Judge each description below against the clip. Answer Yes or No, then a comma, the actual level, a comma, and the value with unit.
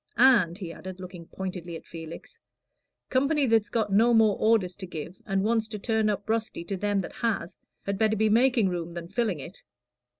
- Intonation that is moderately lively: Yes, average, 3.7 semitones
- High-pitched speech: Yes, high, 205 Hz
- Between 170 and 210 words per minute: Yes, average, 195 wpm